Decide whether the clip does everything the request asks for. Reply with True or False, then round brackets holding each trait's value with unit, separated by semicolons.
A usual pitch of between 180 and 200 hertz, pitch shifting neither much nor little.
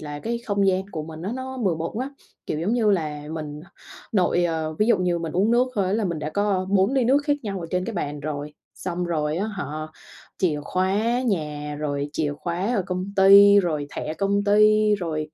True (185 Hz; 4.8 semitones)